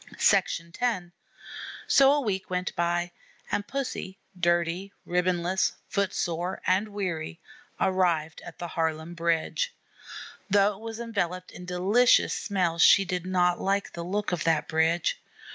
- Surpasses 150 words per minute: No, average, 140 wpm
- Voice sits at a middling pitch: Yes, medium, 180 Hz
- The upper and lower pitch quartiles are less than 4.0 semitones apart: Yes, average, 2.7 semitones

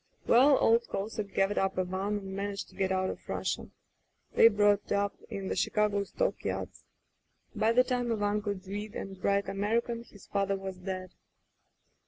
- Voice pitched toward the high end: Yes, high, 200 Hz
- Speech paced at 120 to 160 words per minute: No, average, 170 wpm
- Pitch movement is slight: Yes, narrow, 2.0 semitones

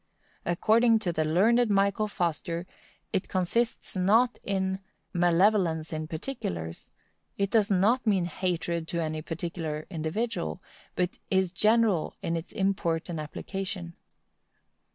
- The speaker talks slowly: Yes, slow, 120 wpm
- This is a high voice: No, medium, 180 Hz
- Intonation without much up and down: No, average, 3.7 semitones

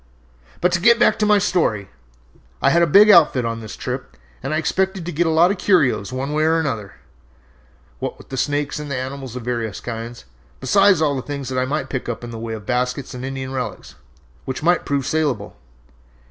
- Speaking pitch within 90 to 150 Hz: Yes, medium, 140 Hz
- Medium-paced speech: No, fast, 210 wpm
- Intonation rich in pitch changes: No, average, 5.0 semitones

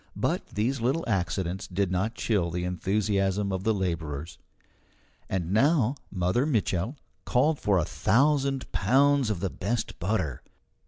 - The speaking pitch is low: Yes, low, 100 Hz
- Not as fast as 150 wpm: Yes, average, 140 wpm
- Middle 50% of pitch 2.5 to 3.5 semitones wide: No, average, 5.3 semitones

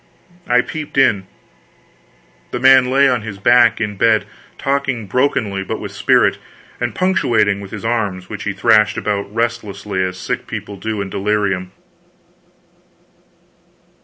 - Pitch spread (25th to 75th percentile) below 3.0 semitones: No, average, 3.6 semitones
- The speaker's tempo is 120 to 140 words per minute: Yes, slow, 135 wpm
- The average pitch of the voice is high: No, low, 105 Hz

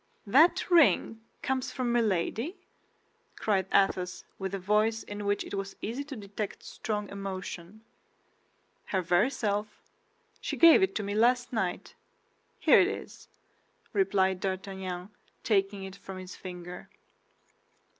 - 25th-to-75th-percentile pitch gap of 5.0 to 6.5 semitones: No, average, 3.1 semitones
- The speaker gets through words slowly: Yes, slow, 125 wpm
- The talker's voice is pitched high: Yes, high, 200 Hz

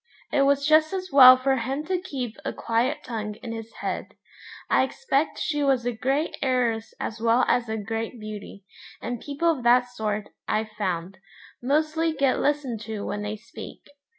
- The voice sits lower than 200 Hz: No, high, 245 Hz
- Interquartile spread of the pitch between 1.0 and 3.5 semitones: No, average, 4.2 semitones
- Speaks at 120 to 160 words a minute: No, average, 180 wpm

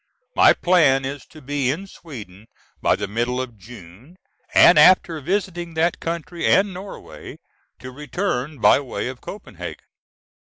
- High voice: No, medium, 145 Hz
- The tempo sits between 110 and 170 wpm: Yes, average, 145 wpm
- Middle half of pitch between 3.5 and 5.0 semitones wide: No, wide, 5.6 semitones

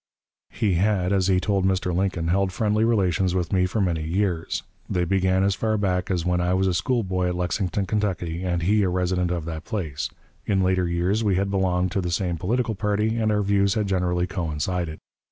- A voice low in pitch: Yes, very low, 95 Hz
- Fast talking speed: Yes, fast, 210 wpm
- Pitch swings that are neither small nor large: No, narrow, 2.1 semitones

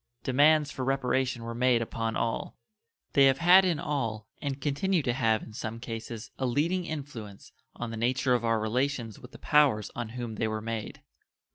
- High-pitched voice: No, low, 125 Hz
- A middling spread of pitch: Yes, average, 3.7 semitones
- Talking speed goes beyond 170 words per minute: Yes, average, 185 wpm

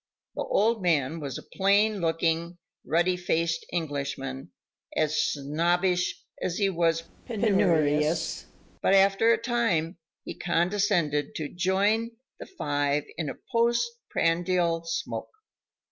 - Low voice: No, medium, 170 Hz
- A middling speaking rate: No, slow, 115 wpm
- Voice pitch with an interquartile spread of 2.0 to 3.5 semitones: No, average, 4.0 semitones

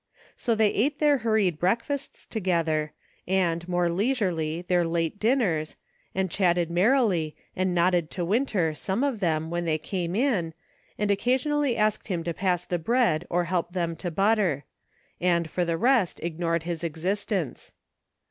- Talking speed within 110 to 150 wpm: No, average, 160 wpm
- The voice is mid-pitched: Yes, medium, 180 Hz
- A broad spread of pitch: No, average, 4.2 semitones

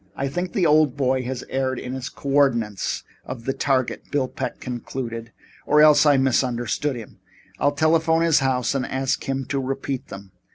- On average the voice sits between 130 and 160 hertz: Yes, low, 135 Hz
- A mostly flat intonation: Yes, narrow, 2.3 semitones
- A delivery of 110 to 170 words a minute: No, average, 180 wpm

